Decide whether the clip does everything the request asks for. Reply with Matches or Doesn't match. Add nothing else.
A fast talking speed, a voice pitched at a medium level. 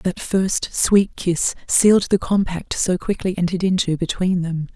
Doesn't match